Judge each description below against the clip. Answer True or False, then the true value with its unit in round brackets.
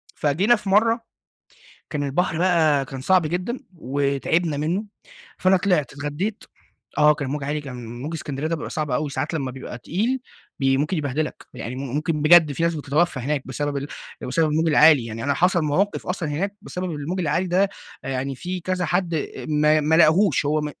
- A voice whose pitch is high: False (155 Hz)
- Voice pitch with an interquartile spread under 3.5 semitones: False (3.8 semitones)